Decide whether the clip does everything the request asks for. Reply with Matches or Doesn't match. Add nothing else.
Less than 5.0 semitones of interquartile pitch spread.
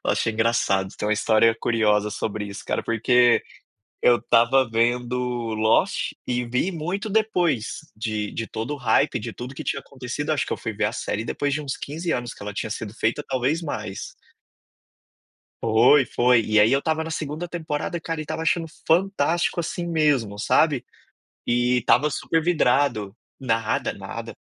Doesn't match